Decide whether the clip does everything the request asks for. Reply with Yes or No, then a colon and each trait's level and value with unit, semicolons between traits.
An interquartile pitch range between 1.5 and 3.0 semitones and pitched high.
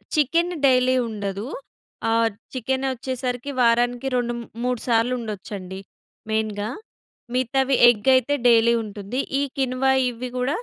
Yes: narrow, 2.6 semitones; high, 245 Hz